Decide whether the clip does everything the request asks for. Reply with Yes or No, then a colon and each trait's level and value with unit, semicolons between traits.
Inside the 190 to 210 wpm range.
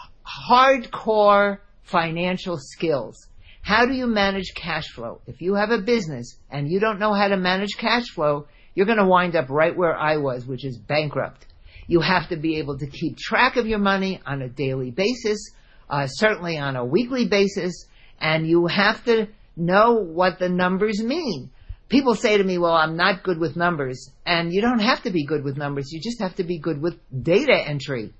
Yes: average, 200 wpm